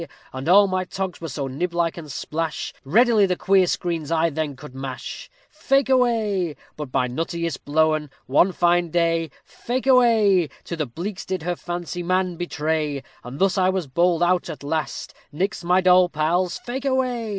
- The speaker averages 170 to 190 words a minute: Yes, average, 175 wpm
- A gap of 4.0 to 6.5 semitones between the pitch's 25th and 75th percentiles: No, average, 3.4 semitones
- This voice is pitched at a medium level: Yes, medium, 175 Hz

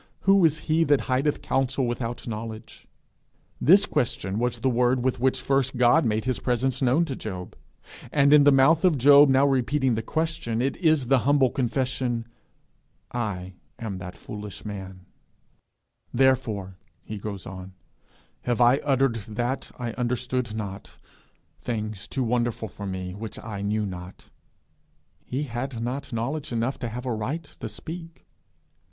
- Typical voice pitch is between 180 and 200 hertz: No, low, 125 Hz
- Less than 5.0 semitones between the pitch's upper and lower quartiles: Yes, average, 3.8 semitones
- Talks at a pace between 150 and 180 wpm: Yes, average, 155 wpm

